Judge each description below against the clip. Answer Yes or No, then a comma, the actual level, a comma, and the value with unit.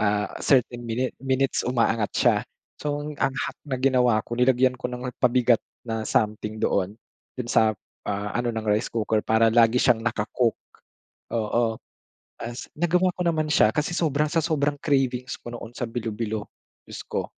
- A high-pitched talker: No, low, 120 Hz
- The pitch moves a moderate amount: Yes, average, 3.0 semitones